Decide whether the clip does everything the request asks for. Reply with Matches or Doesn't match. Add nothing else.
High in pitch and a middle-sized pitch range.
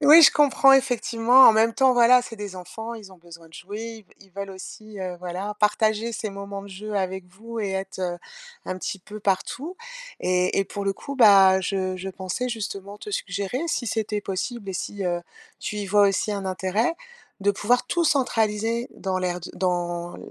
Matches